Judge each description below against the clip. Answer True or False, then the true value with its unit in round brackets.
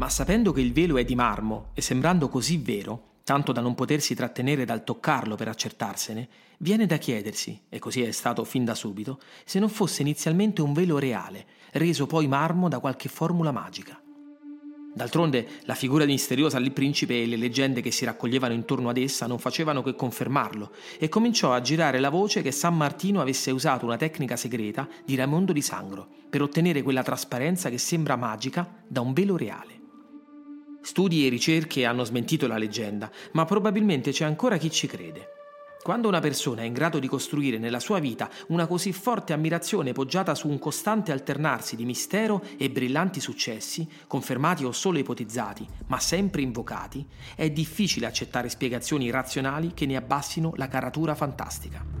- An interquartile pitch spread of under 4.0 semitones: False (5.2 semitones)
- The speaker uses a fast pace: True (175 wpm)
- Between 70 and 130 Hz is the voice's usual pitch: False (140 Hz)